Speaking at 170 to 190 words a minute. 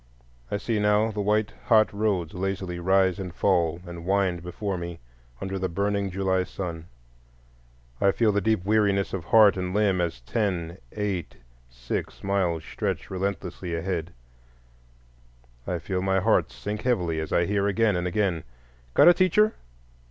No: average, 155 wpm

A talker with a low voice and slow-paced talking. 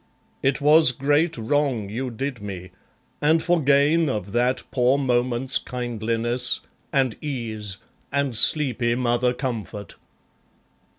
Yes: low, 125 Hz; slow, 115 wpm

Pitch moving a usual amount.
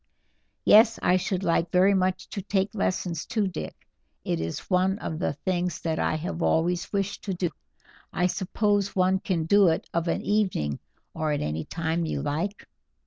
Yes: average, 3.3 semitones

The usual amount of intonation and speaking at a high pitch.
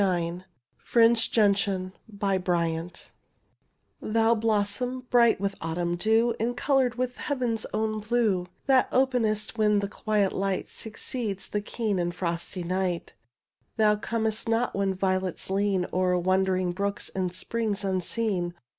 Yes: average, 3.5 semitones; high, 205 Hz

